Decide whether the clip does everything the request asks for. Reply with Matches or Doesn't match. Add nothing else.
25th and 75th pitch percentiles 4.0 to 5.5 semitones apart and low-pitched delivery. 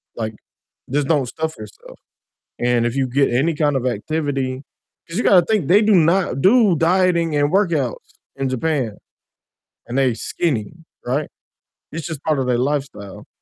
Doesn't match